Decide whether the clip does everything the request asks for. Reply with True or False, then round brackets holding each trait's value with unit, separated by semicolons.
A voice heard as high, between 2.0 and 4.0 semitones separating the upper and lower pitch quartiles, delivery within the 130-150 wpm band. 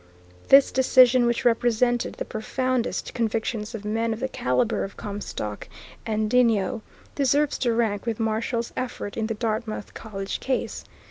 True (230 Hz; 2.4 semitones; 145 wpm)